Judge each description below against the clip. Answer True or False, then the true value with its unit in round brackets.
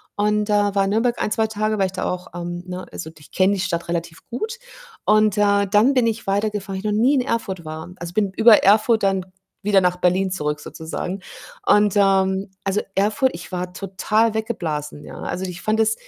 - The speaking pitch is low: False (195 Hz)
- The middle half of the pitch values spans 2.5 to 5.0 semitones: True (2.9 semitones)